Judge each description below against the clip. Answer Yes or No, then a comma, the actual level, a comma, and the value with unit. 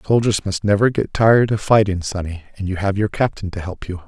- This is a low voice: Yes, low, 100 Hz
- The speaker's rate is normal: No, fast, 235 wpm